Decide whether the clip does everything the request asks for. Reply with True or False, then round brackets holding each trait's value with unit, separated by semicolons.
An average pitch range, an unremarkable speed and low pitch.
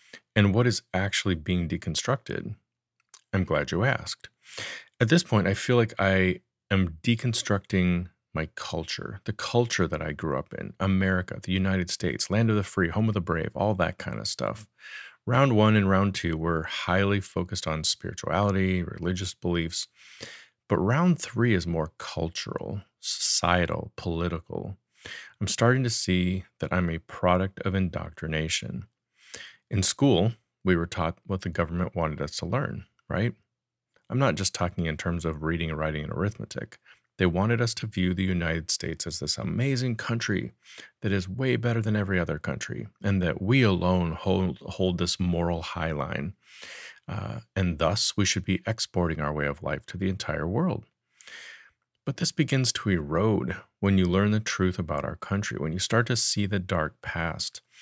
True (3.8 semitones; 170 wpm; 95 Hz)